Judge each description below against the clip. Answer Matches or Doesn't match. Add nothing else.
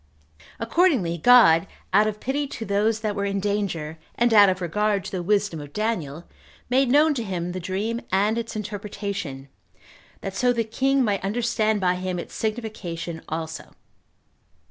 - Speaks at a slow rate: Doesn't match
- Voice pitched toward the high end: Matches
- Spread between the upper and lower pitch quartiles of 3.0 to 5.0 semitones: Matches